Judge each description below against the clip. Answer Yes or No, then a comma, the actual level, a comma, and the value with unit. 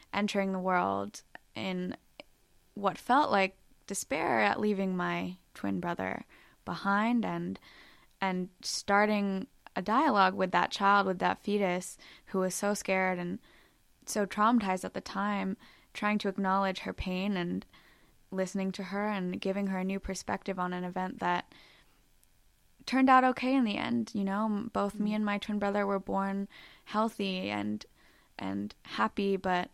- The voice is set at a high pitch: Yes, high, 195 Hz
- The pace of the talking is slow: No, average, 150 wpm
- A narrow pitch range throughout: Yes, narrow, 1.9 semitones